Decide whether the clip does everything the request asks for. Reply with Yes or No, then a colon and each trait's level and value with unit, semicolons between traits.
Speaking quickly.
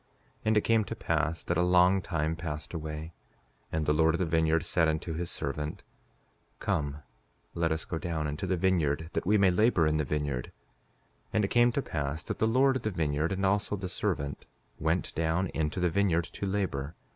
Yes: fast, 210 wpm